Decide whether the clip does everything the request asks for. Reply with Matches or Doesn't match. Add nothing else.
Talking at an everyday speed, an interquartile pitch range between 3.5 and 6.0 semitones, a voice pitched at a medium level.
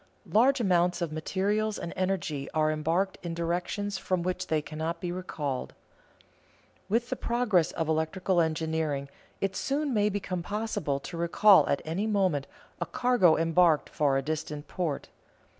Matches